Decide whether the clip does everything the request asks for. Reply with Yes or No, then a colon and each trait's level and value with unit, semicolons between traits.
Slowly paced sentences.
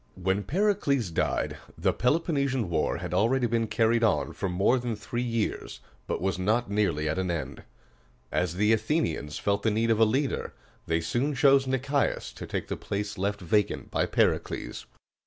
No: average, 175 wpm